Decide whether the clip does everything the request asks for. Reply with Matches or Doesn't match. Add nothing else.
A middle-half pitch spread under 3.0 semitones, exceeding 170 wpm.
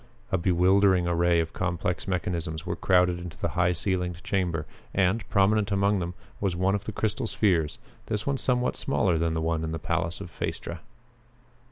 Matches